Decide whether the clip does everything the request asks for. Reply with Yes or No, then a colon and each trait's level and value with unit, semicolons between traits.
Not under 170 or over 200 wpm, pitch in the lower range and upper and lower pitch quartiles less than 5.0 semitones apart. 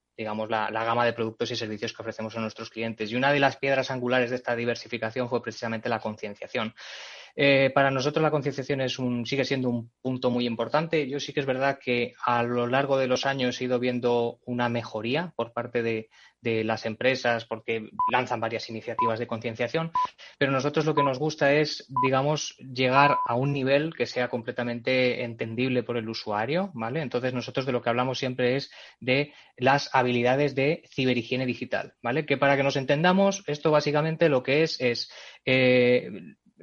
Yes: fast, 190 wpm; low, 125 Hz; average, 2.9 semitones